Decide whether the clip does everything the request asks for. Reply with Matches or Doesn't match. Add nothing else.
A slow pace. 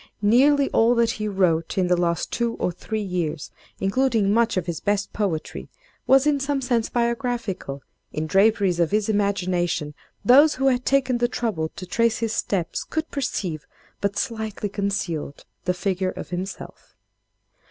Doesn't match